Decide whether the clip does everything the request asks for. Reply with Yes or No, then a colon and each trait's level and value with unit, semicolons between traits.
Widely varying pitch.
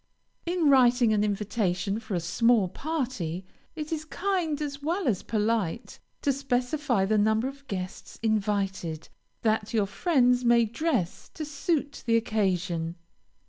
Yes: wide, 5.9 semitones